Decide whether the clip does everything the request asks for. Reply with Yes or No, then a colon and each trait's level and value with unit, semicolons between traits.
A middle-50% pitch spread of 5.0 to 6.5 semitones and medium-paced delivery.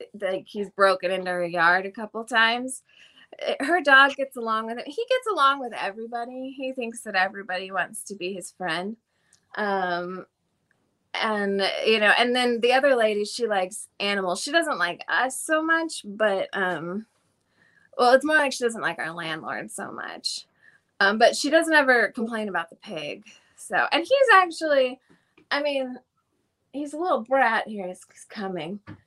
Yes: wide, 5.5 semitones; average, 170 wpm